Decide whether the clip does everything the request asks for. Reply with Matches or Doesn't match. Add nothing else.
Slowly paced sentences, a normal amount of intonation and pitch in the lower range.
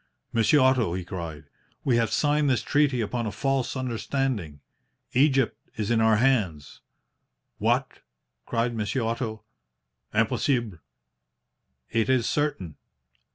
Matches